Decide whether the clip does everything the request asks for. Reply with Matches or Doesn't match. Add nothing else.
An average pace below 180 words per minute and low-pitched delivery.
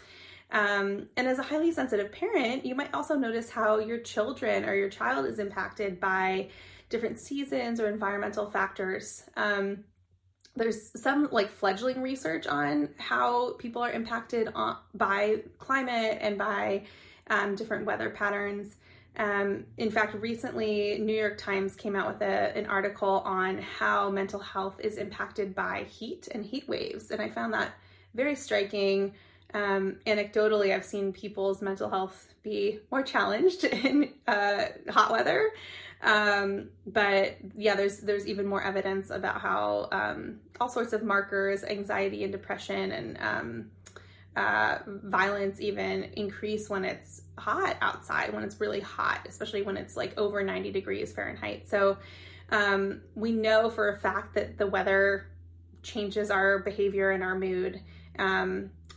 Doesn't match